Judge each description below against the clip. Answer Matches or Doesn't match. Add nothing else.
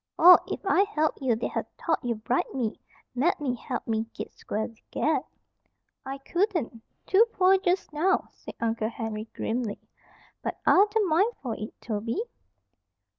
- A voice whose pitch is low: Doesn't match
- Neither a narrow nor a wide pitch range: Doesn't match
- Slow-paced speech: Doesn't match